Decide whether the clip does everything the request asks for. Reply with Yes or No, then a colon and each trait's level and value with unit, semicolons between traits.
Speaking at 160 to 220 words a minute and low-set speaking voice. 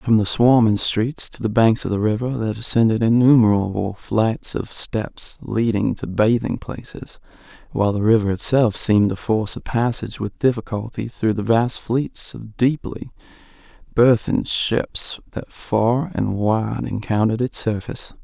No: average, 150 wpm; low, 110 Hz